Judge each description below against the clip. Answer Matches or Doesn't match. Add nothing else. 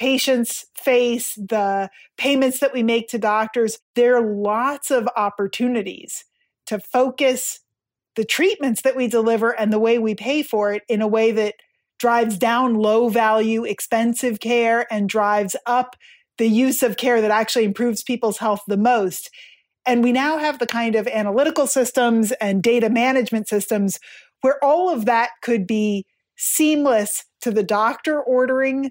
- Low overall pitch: Doesn't match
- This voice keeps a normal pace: Matches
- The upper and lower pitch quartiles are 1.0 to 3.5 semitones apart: Matches